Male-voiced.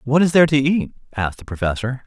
Yes: male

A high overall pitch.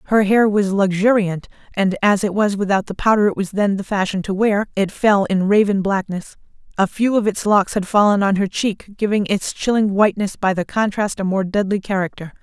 Yes: high, 200 Hz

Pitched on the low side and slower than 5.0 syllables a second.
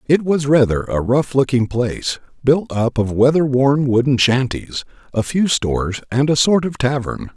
Yes: low, 130 Hz; 4.7 syllables/s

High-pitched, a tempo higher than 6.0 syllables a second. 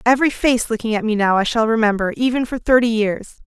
Yes: high, 230 Hz; 6.2 syllables/s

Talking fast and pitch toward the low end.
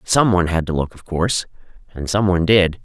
No: average, 190 wpm; very low, 90 Hz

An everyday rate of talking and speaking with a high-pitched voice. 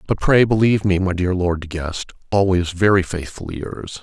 No: average, 195 wpm; very low, 90 Hz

